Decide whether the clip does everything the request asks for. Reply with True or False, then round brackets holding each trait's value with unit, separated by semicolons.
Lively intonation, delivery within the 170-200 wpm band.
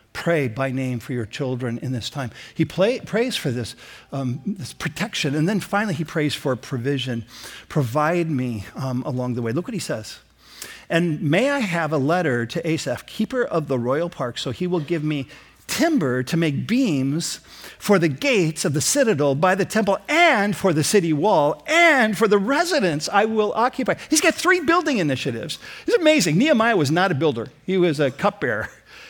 True (7.5 semitones; 190 wpm)